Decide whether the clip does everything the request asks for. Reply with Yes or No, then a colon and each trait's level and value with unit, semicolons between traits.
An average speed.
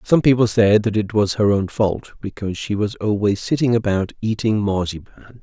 Yes: average, 190 wpm